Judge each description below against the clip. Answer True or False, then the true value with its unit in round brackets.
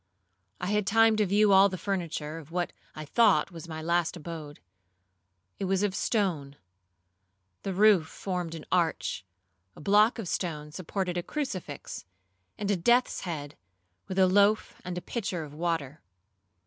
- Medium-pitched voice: True (180 Hz)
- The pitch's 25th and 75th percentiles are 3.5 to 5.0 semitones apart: True (3.8 semitones)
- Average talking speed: True (155 wpm)